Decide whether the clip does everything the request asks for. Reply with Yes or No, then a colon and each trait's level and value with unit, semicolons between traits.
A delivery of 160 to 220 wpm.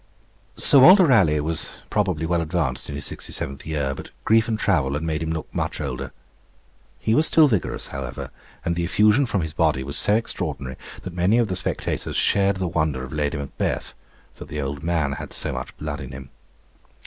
Yes: average, 200 wpm